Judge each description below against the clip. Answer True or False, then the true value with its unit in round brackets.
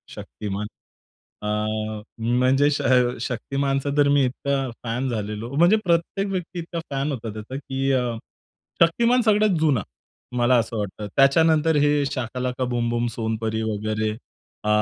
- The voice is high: False (130 Hz)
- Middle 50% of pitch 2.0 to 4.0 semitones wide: False (4.9 semitones)